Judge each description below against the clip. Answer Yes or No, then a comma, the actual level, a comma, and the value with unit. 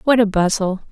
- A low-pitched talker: No, high, 205 Hz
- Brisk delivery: No, average, 195 wpm